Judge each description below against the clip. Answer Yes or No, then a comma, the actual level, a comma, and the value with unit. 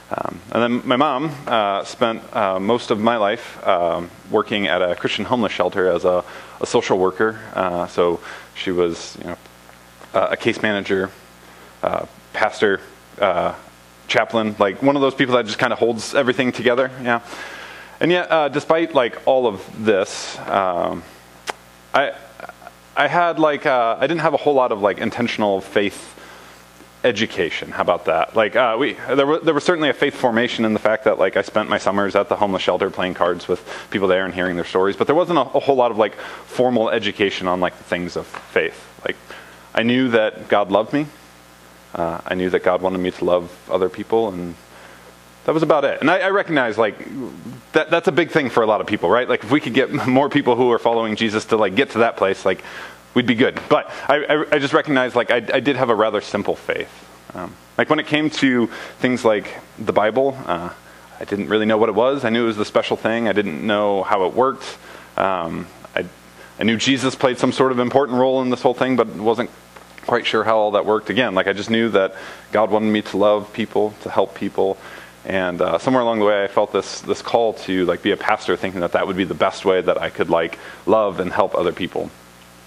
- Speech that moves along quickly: Yes, fast, 225 wpm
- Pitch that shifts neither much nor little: No, wide, 6.2 semitones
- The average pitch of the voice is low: Yes, low, 105 Hz